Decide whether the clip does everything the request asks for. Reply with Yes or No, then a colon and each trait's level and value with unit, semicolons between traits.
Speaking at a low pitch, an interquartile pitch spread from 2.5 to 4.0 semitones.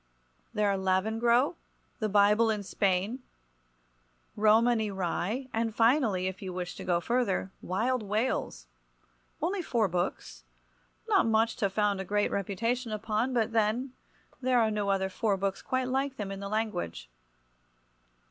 No: high, 210 Hz; average, 3.5 semitones